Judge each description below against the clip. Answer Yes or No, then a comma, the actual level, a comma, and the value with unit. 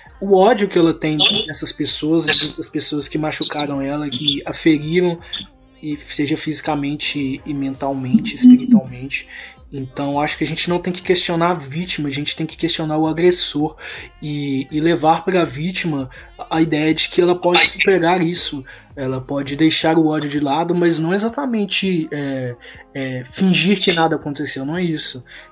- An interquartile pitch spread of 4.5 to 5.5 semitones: No, average, 3.3 semitones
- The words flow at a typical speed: Yes, average, 170 wpm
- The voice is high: No, medium, 155 Hz